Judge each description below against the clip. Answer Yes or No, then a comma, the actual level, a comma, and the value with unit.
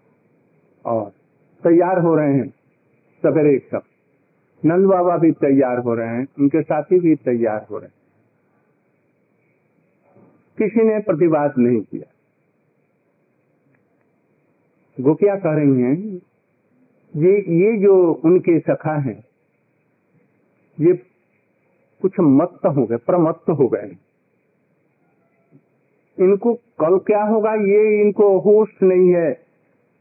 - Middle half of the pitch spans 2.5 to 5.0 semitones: No, wide, 5.4 semitones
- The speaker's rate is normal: No, slow, 105 wpm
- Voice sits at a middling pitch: Yes, medium, 170 Hz